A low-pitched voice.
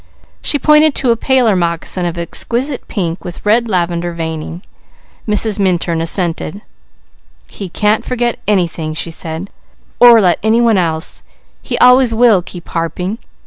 No: high, 190 Hz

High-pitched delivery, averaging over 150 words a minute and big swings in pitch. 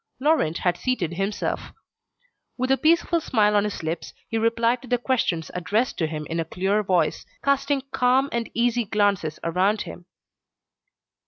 Yes: high, 210 Hz; average, 160 wpm; wide, 6.0 semitones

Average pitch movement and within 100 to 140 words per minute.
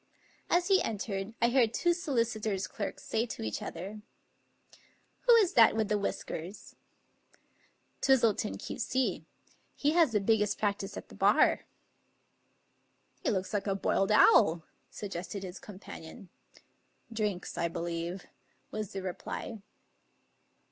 Yes: average, 3.5 semitones; slow, 135 wpm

